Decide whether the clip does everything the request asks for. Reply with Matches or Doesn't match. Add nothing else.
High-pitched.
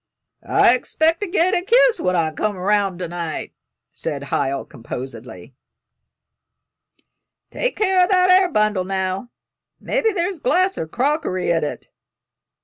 Matches